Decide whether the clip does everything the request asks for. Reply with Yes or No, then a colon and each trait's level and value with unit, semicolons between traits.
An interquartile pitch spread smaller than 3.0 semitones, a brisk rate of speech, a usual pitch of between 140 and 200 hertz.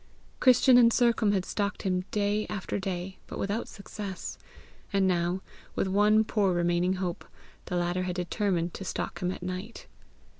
No: narrow, 2.6 semitones; average, 160 wpm; high, 190 Hz